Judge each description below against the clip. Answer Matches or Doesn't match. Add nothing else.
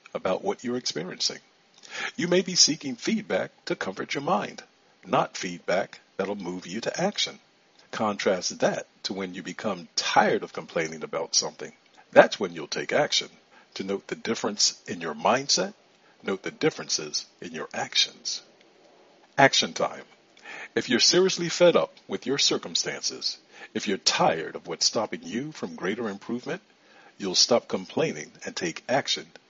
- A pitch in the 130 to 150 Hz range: Doesn't match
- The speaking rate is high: Doesn't match